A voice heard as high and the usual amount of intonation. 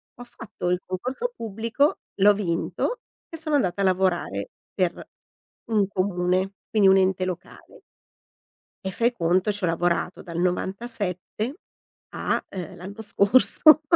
Yes: high, 195 Hz; average, 3.9 semitones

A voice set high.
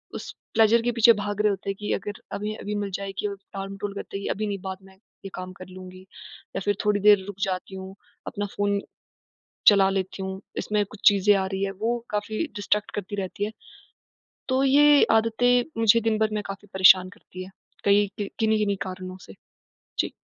Yes: high, 205 Hz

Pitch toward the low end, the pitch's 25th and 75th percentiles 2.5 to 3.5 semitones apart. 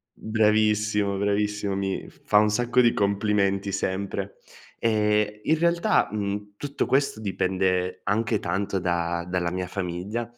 No: low, 100 Hz; narrow, 2.0 semitones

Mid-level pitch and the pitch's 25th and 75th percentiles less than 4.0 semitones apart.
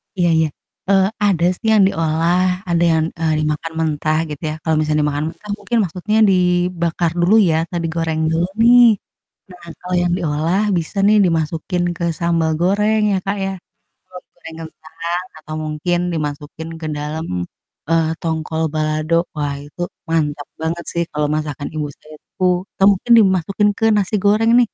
Yes: medium, 170 Hz; average, 2.8 semitones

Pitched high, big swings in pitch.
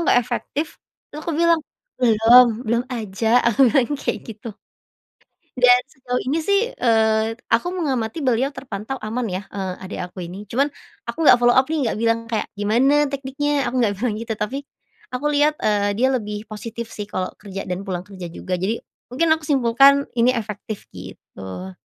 No: high, 230 Hz; average, 4.5 semitones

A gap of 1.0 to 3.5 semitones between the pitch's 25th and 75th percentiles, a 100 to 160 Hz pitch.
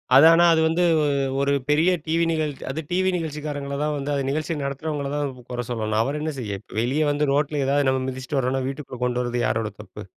Yes: average, 2.8 semitones; medium, 140 Hz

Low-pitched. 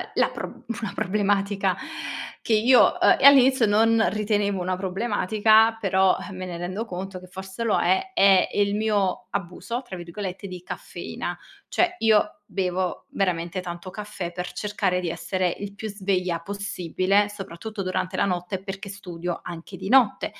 No: high, 195 Hz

